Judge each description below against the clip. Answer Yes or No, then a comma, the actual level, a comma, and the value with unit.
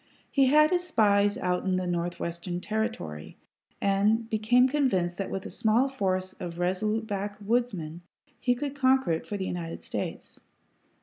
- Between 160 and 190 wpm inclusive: No, average, 150 wpm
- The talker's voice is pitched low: No, high, 205 Hz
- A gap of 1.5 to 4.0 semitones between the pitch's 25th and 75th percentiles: No, wide, 5.4 semitones